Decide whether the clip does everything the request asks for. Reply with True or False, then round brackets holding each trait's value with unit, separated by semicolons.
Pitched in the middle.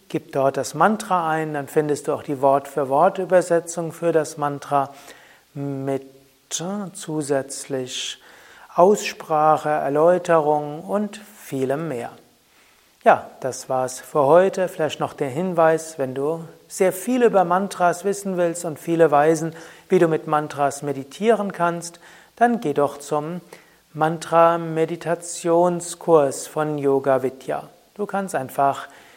True (160 Hz)